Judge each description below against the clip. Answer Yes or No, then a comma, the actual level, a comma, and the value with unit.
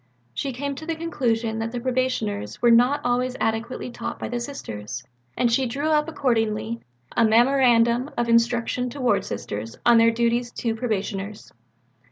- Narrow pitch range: Yes, narrow, 2.3 semitones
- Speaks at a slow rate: No, average, 165 wpm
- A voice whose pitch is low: No, high, 235 Hz